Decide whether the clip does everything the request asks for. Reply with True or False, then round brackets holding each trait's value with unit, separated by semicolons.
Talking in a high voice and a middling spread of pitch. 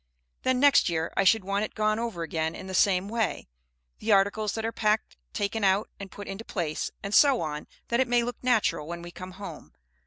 True (200 Hz; 3.5 semitones)